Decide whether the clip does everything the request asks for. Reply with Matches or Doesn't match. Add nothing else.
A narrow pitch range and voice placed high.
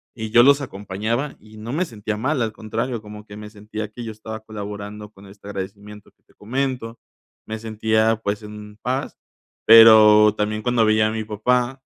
Doesn't match